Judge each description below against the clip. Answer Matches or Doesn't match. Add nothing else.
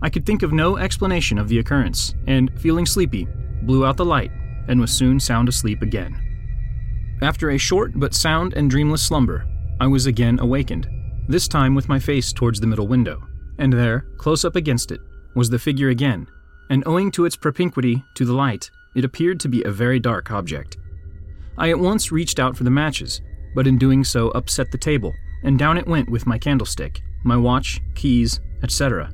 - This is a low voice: Matches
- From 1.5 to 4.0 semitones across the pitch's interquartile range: Matches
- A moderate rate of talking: Matches